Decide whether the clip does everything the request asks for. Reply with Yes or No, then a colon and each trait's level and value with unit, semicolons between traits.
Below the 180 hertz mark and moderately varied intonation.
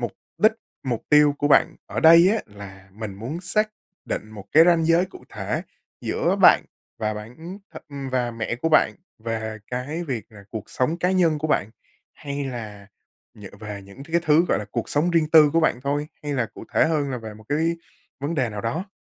No: medium, 140 Hz; wide, 6.8 semitones